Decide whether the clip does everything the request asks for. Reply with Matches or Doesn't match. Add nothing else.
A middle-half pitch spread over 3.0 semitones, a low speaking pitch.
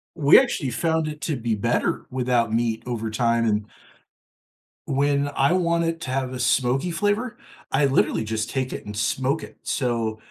Matches